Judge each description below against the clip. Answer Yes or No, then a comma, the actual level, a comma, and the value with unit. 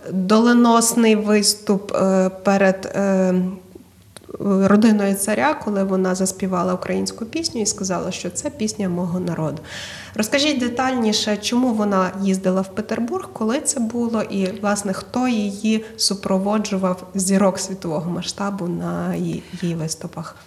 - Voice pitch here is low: No, high, 195 Hz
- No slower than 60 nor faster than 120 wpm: Yes, average, 110 wpm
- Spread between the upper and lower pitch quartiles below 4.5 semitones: Yes, average, 2.8 semitones